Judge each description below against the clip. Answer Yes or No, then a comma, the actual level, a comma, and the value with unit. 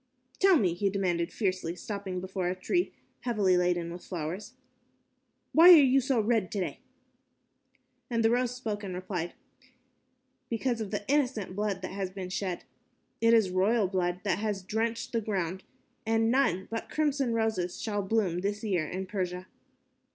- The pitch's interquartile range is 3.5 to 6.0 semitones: Yes, average, 3.8 semitones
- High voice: Yes, high, 200 Hz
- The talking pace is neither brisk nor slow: Yes, average, 160 wpm